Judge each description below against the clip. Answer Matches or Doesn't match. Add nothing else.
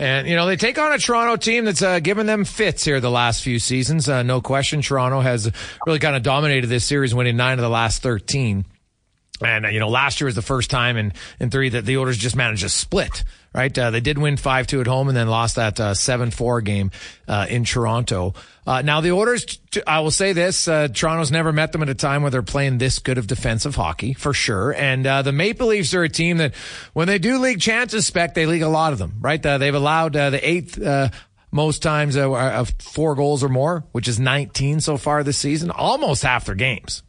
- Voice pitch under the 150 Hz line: Matches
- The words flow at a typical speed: Doesn't match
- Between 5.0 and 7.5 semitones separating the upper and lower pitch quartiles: Doesn't match